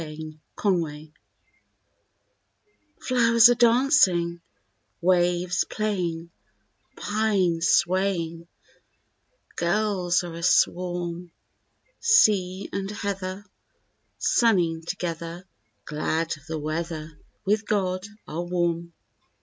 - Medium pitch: Yes, medium, 175 Hz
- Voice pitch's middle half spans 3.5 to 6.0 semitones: No, average, 3.1 semitones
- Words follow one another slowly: Yes, slow, 80 wpm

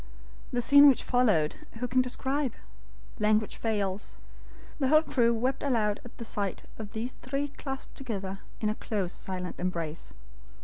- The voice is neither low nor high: No, high, 225 Hz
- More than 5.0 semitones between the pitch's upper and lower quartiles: No, average, 4.5 semitones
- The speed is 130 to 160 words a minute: Yes, average, 150 wpm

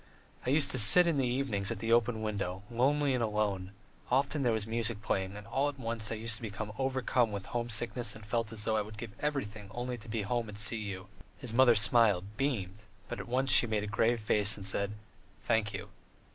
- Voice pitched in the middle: No, low, 115 Hz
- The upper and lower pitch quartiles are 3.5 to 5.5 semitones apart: No, average, 3.0 semitones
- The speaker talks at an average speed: No, fast, 230 wpm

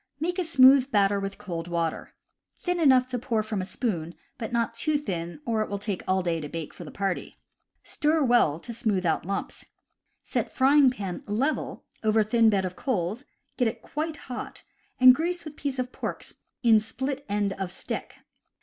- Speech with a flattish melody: No, wide, 5.5 semitones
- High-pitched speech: Yes, high, 225 Hz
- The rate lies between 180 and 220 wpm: Yes, average, 195 wpm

